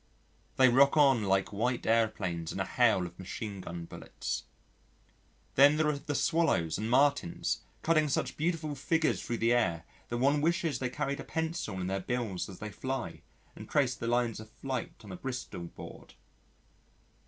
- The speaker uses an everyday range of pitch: No, wide, 6.4 semitones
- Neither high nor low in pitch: No, low, 120 Hz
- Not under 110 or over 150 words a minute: No, average, 175 wpm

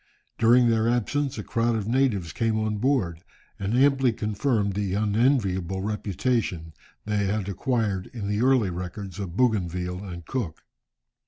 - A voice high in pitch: No, low, 105 Hz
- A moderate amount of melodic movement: Yes, average, 4.0 semitones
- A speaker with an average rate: Yes, average, 145 wpm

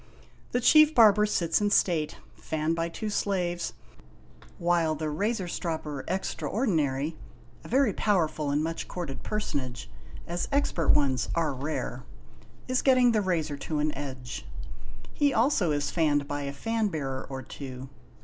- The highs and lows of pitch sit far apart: Yes, wide, 6.2 semitones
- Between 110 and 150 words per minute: Yes, average, 145 wpm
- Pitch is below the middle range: No, medium, 165 Hz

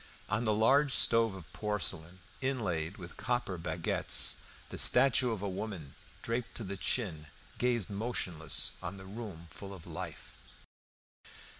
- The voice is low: Yes, low, 100 Hz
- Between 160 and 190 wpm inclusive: No, average, 140 wpm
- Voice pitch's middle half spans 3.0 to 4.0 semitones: No, average, 4.8 semitones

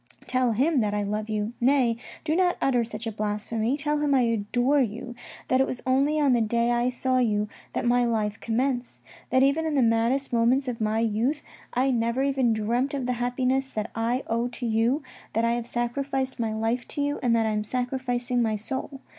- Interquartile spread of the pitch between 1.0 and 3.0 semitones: Yes, average, 2.7 semitones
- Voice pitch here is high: Yes, high, 245 Hz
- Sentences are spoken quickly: Yes, fast, 215 wpm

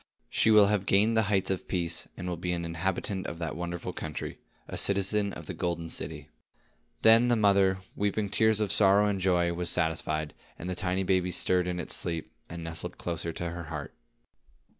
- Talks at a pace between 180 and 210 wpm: Yes, average, 200 wpm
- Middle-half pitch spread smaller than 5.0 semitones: Yes, average, 2.8 semitones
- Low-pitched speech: Yes, very low, 90 Hz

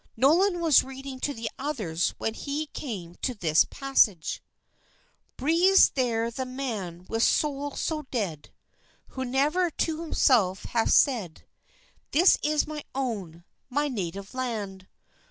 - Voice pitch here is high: Yes, very high, 255 Hz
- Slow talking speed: Yes, slow, 130 wpm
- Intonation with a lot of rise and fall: Yes, wide, 6.1 semitones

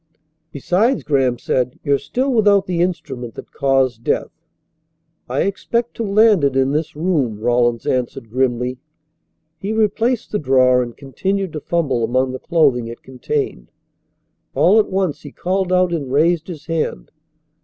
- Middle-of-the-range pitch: Yes, medium, 150 Hz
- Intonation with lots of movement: Yes, wide, 7.0 semitones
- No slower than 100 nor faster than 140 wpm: No, average, 155 wpm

